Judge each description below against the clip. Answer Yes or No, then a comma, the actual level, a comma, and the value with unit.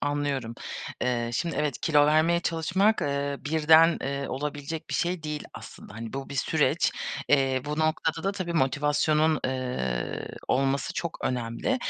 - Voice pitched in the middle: Yes, medium, 145 Hz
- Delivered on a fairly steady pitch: No, average, 3.3 semitones